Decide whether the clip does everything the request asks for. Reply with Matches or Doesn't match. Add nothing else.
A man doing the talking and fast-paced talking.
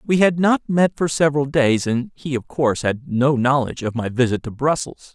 Matches